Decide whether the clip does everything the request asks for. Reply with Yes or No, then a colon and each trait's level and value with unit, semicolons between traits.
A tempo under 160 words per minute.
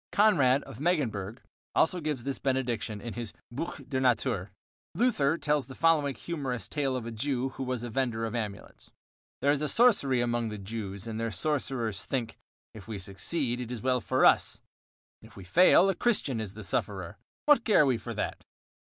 No: average, 185 wpm